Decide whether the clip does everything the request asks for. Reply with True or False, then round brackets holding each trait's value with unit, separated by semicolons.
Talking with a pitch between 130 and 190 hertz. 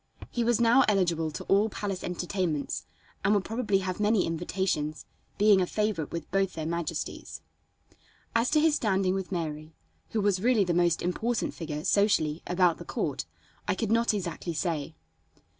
True (185 Hz)